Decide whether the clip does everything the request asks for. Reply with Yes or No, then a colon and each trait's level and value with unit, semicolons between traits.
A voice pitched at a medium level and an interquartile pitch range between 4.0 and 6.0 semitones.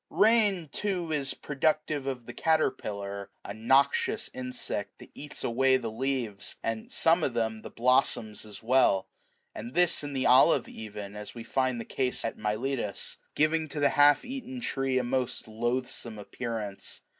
No: low, 130 Hz; average, 4.7 semitones